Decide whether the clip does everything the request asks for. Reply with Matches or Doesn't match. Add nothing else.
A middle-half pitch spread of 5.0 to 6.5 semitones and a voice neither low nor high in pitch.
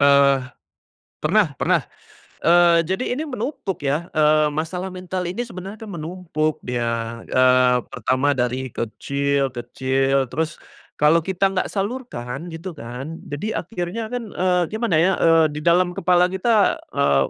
Matches